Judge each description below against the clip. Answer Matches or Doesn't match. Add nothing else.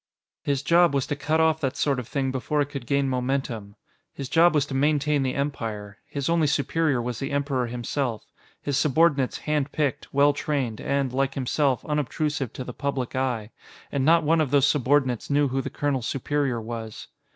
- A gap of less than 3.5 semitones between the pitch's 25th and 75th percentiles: Matches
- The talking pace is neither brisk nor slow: Matches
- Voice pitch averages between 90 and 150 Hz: Matches